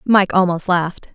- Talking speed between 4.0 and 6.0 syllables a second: Yes, 5.0 syllables/s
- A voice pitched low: No, medium, 180 Hz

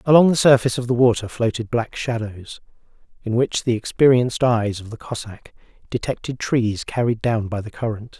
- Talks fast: No, average, 175 wpm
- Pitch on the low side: Yes, low, 115 Hz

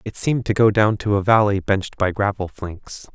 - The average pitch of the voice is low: Yes, low, 100 Hz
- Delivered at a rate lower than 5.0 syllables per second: No, 5.3 syllables/s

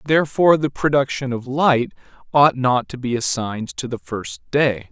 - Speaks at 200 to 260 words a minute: No, average, 170 wpm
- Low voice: Yes, low, 130 Hz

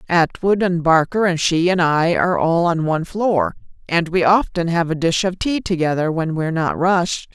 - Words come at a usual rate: No, fast, 210 wpm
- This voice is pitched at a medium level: Yes, medium, 170 Hz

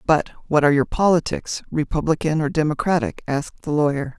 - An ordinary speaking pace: Yes, average, 145 wpm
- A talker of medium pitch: Yes, medium, 150 Hz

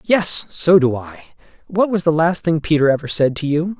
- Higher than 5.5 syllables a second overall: No, 4.9 syllables/s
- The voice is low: No, medium, 160 Hz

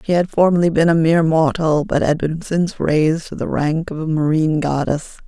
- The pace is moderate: No, fast, 215 wpm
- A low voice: No, medium, 160 Hz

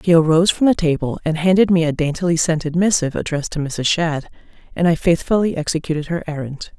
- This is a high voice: No, medium, 165 Hz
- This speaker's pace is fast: No, average, 195 wpm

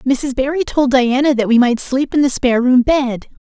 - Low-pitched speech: No, very high, 260 Hz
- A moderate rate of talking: No, fast, 225 wpm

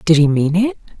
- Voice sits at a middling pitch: Yes, medium, 175 Hz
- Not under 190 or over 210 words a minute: No, fast, 240 wpm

